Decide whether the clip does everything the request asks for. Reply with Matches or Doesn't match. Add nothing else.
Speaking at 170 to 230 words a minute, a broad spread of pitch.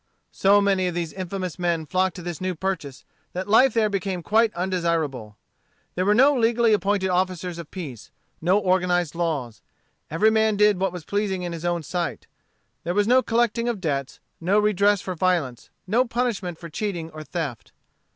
Doesn't match